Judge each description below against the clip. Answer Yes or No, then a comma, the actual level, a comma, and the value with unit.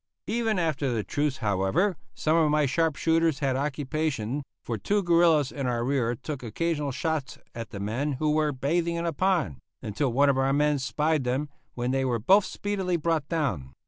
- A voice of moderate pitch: Yes, medium, 145 Hz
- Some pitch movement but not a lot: Yes, average, 4.3 semitones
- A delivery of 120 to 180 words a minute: No, average, 190 wpm